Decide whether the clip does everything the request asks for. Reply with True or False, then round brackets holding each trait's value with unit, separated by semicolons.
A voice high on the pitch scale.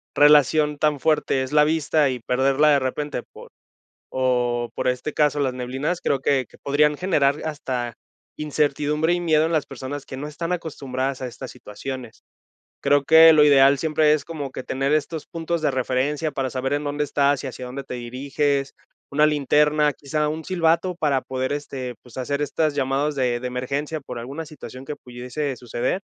False (145 Hz)